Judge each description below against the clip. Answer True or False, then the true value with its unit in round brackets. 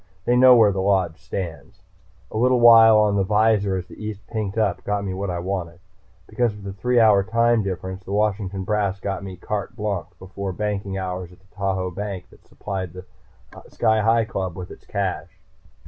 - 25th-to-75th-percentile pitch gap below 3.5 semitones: True (2.4 semitones)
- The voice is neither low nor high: False (100 Hz)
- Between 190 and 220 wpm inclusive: True (195 wpm)